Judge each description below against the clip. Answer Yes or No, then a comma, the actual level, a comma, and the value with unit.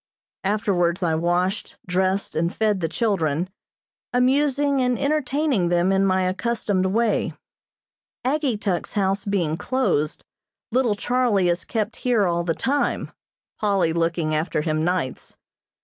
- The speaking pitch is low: No, high, 195 Hz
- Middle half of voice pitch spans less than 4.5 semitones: No, wide, 5.6 semitones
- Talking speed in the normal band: No, slow, 125 wpm